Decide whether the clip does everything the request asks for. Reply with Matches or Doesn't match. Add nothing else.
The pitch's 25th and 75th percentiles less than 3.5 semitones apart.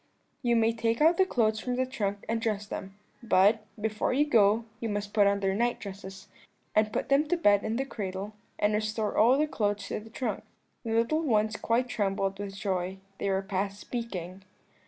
Matches